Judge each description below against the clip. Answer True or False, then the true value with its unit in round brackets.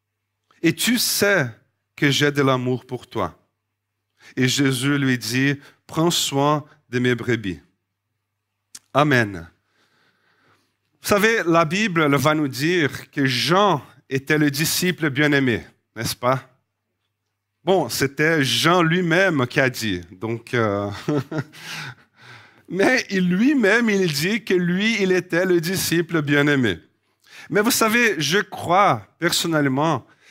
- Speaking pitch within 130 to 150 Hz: True (140 Hz)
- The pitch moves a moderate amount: False (6.5 semitones)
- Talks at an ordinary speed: False (120 wpm)